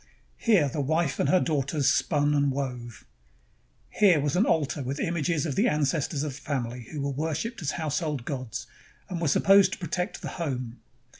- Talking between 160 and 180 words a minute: No, average, 190 wpm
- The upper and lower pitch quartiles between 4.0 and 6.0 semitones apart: No, average, 3.3 semitones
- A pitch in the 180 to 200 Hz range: No, medium, 145 Hz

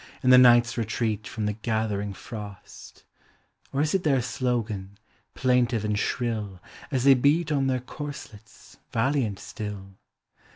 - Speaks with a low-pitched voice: Yes, low, 120 Hz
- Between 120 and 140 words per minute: Yes, slow, 135 wpm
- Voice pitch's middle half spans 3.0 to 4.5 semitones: Yes, average, 3.7 semitones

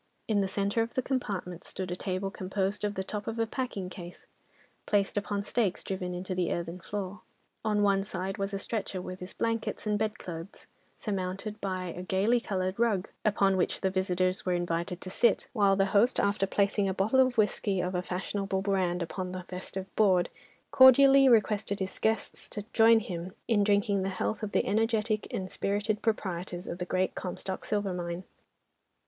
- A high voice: Yes, high, 195 Hz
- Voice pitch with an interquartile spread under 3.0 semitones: Yes, narrow, 2.4 semitones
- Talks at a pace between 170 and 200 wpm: Yes, average, 185 wpm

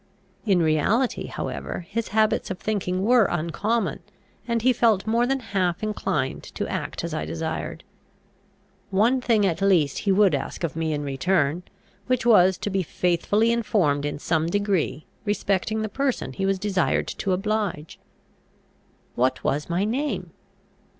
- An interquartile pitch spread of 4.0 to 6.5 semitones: Yes, average, 4.9 semitones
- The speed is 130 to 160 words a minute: Yes, average, 150 wpm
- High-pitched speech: Yes, high, 195 Hz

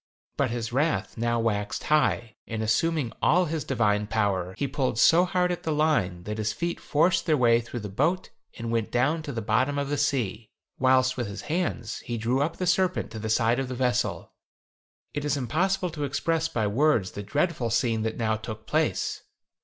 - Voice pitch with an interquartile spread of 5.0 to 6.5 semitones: Yes, wide, 5.5 semitones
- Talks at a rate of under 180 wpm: No, average, 200 wpm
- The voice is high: No, low, 125 Hz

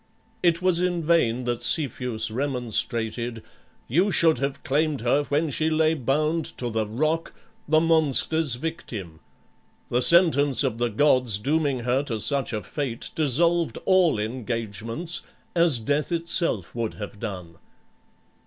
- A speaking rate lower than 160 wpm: Yes, slow, 135 wpm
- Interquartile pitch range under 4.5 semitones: No, wide, 5.6 semitones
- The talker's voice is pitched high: No, medium, 140 Hz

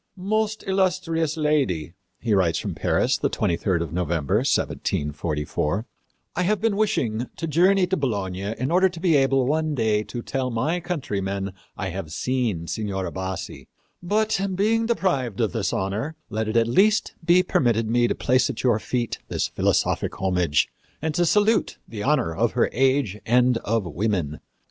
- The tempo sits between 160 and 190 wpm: Yes, average, 165 wpm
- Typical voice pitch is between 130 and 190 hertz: No, low, 120 Hz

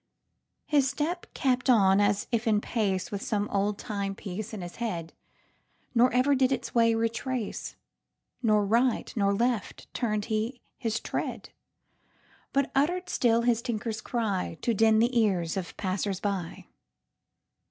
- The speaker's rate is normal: No, slow, 120 wpm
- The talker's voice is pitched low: No, high, 225 Hz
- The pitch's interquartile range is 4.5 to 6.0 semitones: No, average, 3.4 semitones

